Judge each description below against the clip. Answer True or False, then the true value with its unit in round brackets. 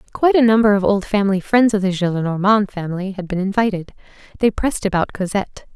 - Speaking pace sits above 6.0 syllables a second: True (6.6 syllables/s)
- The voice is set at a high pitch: True (200 Hz)